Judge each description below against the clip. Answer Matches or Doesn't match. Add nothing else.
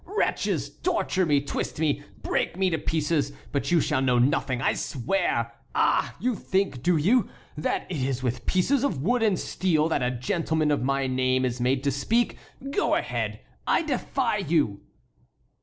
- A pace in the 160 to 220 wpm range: Matches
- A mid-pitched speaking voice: Matches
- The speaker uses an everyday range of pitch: Doesn't match